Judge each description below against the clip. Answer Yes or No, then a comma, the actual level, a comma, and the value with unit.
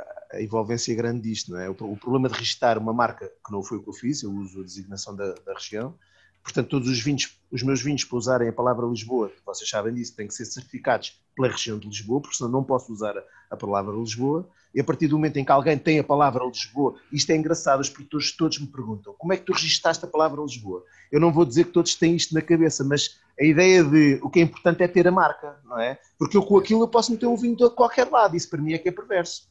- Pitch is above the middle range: No, medium, 145 Hz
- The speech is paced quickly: Yes, fast, 260 wpm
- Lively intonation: Yes, wide, 6.0 semitones